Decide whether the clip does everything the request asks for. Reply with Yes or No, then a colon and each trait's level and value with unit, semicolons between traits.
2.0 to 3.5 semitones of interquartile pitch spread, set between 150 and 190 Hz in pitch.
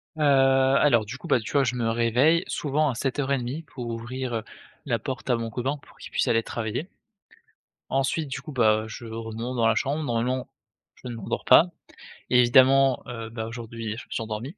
No: average, 2.9 semitones; low, 125 Hz